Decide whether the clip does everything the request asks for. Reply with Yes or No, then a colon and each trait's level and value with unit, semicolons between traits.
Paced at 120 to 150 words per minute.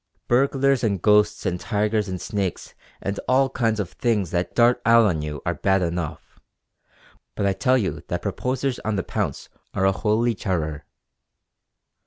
No: average, 165 wpm